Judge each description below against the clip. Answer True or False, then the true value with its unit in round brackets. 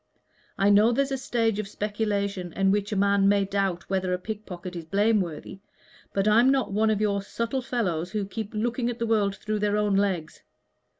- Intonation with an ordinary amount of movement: False (2.2 semitones)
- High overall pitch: True (205 Hz)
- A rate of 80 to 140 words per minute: False (195 wpm)